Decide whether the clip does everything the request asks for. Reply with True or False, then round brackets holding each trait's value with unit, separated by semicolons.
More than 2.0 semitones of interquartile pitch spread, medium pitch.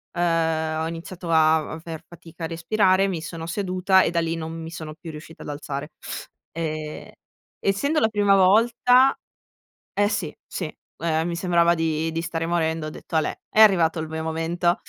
True (2.5 semitones; 165 Hz)